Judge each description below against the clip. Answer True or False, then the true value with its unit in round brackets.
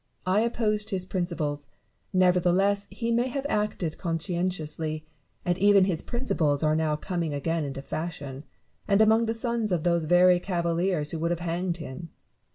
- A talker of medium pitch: True (175 Hz)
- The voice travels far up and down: False (4.1 semitones)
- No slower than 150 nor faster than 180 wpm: True (165 wpm)